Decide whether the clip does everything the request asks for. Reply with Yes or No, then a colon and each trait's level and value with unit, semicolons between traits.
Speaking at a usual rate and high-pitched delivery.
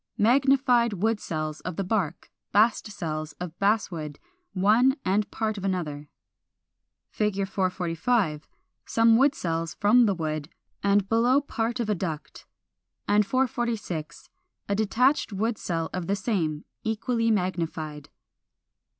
No: slow, 125 wpm; high, 200 Hz